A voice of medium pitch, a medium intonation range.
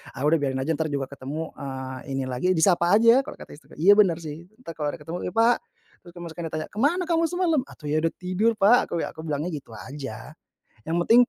No: medium, 165 Hz; wide, 6.3 semitones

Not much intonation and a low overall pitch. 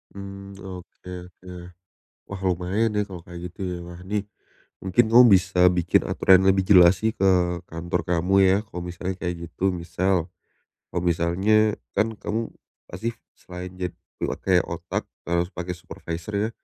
Yes: narrow, 1.9 semitones; very low, 90 Hz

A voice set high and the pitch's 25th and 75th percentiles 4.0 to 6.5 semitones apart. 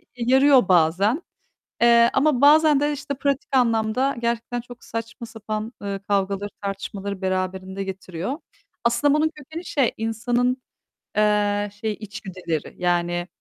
Yes: high, 225 Hz; average, 4.7 semitones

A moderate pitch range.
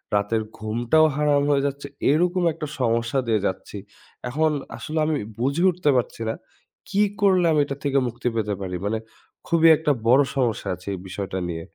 No: wide, 5.8 semitones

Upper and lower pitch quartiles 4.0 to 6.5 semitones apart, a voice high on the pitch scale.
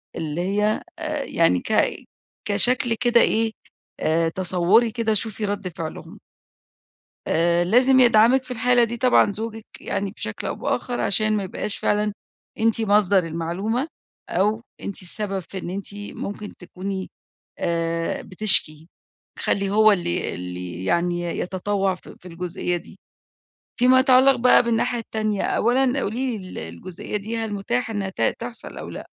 Yes: average, 4.5 semitones; high, 205 Hz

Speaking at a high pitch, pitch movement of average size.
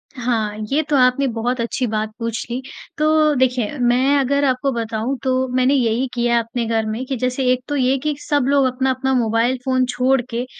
No: very high, 255 Hz; narrow, 2.3 semitones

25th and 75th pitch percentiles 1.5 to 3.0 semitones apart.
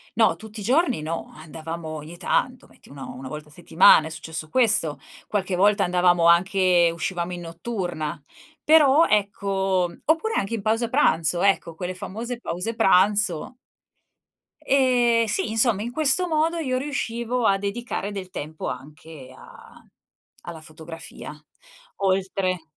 No: wide, 5.9 semitones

